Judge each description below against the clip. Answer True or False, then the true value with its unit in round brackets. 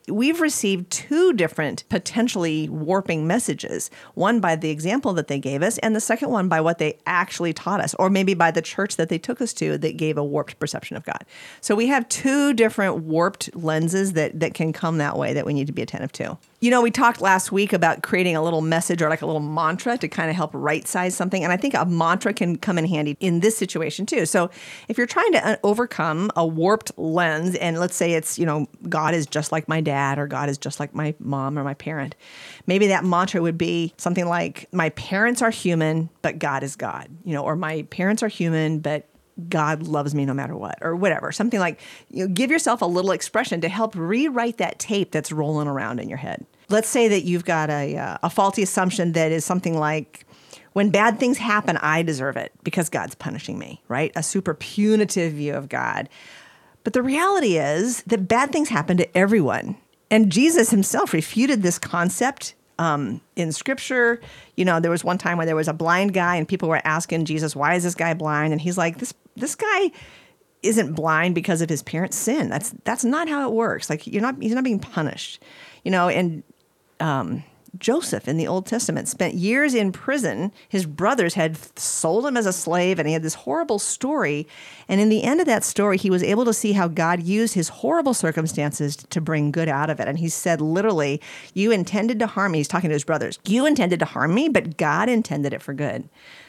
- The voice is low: False (175 Hz)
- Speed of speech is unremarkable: False (220 wpm)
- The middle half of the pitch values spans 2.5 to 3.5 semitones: False (5.3 semitones)